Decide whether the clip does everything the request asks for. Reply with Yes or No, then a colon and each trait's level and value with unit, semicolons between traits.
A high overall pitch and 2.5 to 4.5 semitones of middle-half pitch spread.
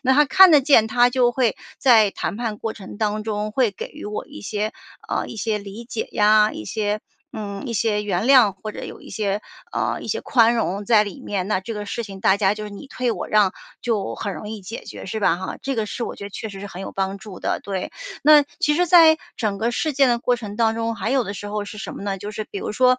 Yes: high, 215 Hz; average, 2.9 semitones